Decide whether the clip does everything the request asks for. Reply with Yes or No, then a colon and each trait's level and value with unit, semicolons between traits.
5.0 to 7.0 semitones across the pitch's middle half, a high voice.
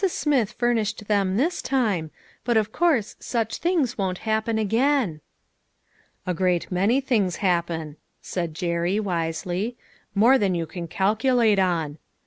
Yes: average, 5.3 semitones; high, 205 Hz